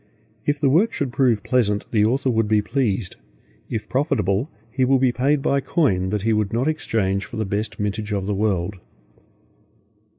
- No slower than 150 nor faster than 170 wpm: No, average, 185 wpm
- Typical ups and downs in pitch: Yes, average, 4.5 semitones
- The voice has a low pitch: Yes, low, 110 Hz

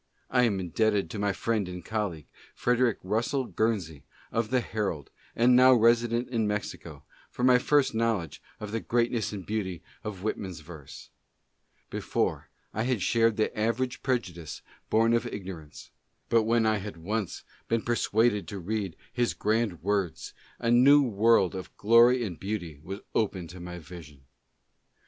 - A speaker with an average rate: Yes, average, 160 wpm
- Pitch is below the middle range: Yes, low, 110 Hz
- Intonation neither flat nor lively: Yes, average, 4.0 semitones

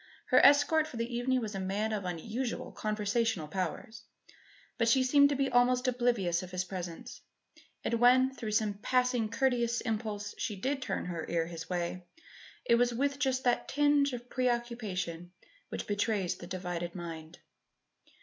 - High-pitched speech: Yes, high, 225 Hz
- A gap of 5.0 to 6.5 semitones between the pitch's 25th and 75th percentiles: Yes, wide, 5.4 semitones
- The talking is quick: No, average, 160 wpm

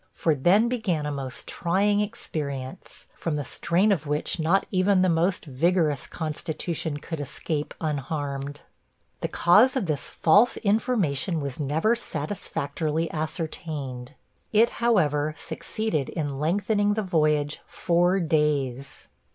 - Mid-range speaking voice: Yes, medium, 160 Hz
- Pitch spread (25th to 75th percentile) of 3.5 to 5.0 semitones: Yes, average, 4.6 semitones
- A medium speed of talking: No, slow, 125 wpm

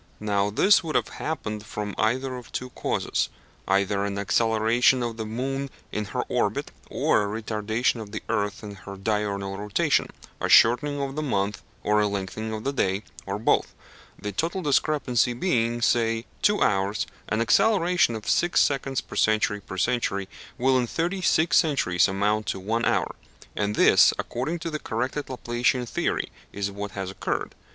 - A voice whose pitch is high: No, low, 110 Hz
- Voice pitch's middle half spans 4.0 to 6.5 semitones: Yes, average, 4.4 semitones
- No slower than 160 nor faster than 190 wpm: Yes, average, 170 wpm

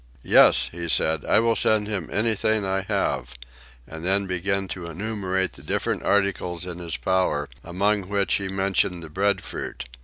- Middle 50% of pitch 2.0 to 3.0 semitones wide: Yes, narrow, 2.6 semitones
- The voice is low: Yes, very low, 95 Hz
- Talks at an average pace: Yes, average, 160 wpm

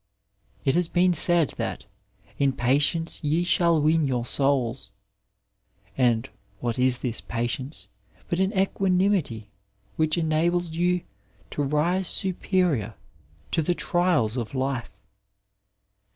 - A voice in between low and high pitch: Yes, medium, 155 Hz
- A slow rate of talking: Yes, slow, 120 wpm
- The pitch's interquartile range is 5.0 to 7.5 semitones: Yes, wide, 5.5 semitones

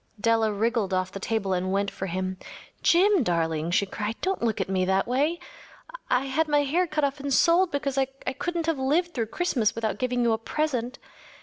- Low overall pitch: No, high, 245 Hz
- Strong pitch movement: Yes, wide, 6.9 semitones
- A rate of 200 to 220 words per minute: Yes, fast, 205 wpm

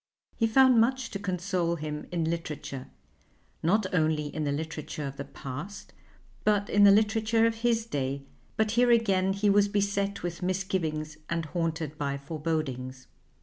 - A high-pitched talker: No, medium, 175 Hz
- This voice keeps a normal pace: Yes, average, 155 wpm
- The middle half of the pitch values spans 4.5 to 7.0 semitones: Yes, average, 5.2 semitones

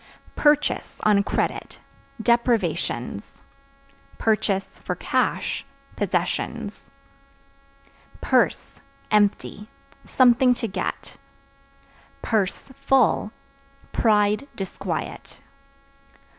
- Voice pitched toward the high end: Yes, high, 215 Hz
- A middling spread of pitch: Yes, average, 3.3 semitones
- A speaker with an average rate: No, slow, 55 wpm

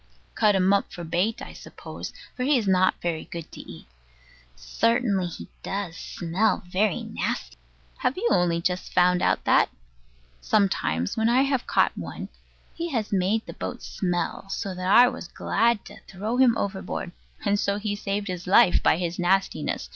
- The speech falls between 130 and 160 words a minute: No, average, 175 wpm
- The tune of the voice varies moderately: Yes, average, 3.8 semitones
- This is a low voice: No, high, 195 Hz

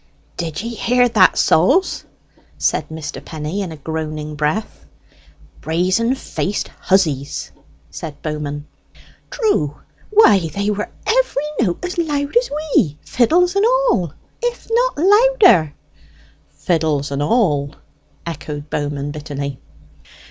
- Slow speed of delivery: Yes, slow, 115 wpm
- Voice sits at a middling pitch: Yes, medium, 180 Hz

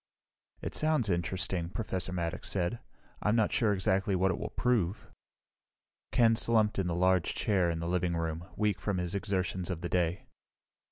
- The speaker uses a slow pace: No, average, 170 wpm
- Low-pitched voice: Yes, very low, 95 Hz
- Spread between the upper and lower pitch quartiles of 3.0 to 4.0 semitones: Yes, average, 3.3 semitones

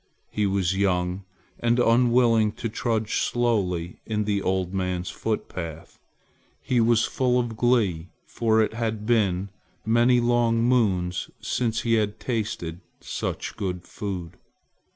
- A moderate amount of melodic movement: Yes, average, 4.0 semitones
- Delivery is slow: Yes, slow, 130 wpm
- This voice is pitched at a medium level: No, low, 110 Hz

